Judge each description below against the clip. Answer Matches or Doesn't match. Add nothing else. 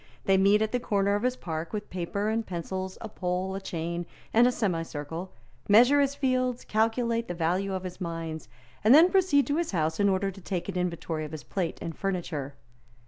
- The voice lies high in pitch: Matches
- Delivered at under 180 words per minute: Doesn't match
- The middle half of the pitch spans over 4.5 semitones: Matches